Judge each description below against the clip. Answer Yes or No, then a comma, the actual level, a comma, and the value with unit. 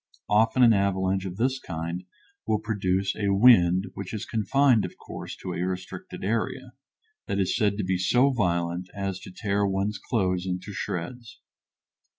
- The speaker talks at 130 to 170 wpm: Yes, average, 160 wpm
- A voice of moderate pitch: No, low, 100 Hz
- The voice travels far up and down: No, average, 3.0 semitones